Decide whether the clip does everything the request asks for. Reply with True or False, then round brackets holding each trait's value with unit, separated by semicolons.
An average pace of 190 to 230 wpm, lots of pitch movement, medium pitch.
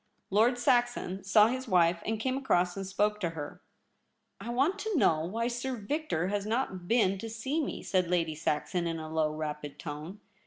False (195 wpm; 6.2 semitones; 200 Hz)